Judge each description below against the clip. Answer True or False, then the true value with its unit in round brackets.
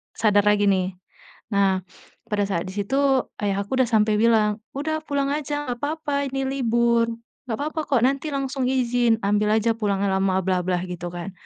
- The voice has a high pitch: True (225 Hz)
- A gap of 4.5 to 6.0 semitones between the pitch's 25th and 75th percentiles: True (5.1 semitones)